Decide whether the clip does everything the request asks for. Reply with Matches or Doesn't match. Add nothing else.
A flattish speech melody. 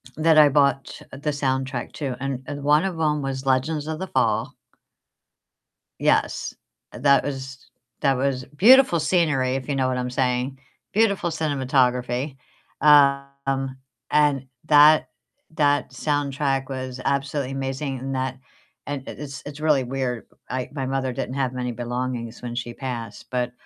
Matches